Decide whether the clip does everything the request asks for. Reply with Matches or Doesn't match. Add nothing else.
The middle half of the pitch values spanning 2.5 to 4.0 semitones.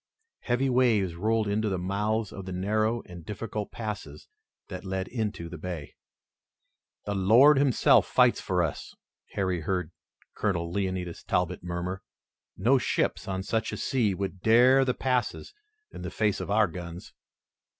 Matches